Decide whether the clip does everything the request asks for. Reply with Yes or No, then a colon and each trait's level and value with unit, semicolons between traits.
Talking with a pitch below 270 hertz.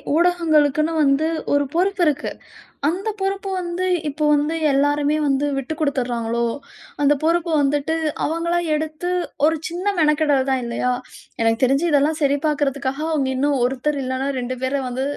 No: very high, 290 Hz